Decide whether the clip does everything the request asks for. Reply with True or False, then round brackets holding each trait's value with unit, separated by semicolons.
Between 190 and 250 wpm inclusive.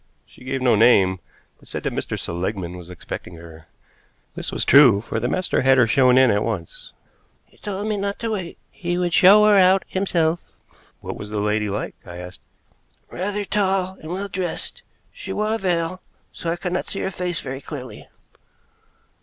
True (195 wpm)